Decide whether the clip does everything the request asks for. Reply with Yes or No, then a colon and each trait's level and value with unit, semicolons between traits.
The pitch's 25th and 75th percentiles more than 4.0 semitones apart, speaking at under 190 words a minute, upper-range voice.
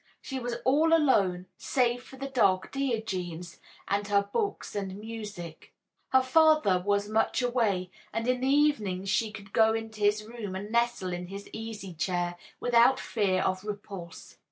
Yes: average, 4.4 semitones; average, 160 wpm; high, 215 Hz